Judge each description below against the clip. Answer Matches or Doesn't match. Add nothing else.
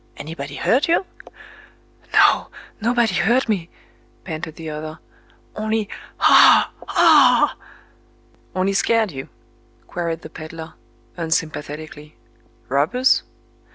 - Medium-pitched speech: Matches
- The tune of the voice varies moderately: Doesn't match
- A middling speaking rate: Doesn't match